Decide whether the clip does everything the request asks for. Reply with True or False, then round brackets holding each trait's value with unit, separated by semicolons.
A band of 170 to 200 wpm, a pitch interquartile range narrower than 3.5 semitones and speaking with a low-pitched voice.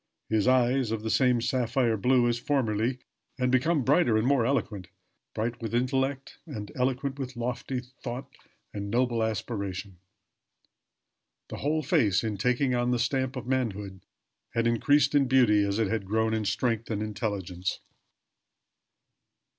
False (145 wpm; 3.1 semitones; 120 Hz)